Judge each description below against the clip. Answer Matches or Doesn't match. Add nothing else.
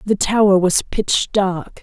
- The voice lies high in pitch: Matches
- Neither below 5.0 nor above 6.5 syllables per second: Doesn't match